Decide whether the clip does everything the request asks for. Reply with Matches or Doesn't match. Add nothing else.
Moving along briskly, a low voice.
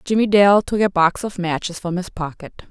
Doesn't match